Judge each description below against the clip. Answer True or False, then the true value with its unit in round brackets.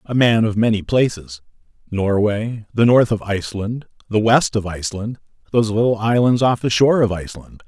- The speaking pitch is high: False (110 Hz)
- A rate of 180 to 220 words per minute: False (165 wpm)